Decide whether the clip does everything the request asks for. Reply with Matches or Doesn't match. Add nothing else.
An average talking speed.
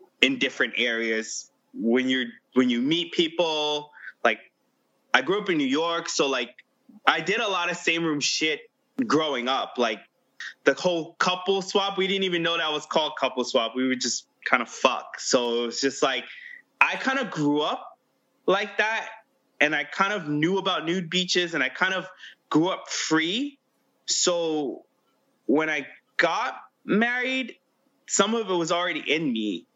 Matches